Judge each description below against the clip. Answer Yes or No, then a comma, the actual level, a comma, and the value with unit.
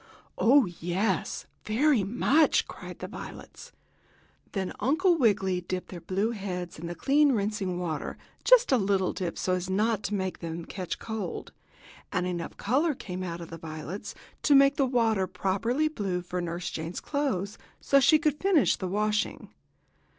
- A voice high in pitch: Yes, high, 200 Hz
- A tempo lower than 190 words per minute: Yes, average, 165 wpm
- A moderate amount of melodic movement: No, wide, 6.1 semitones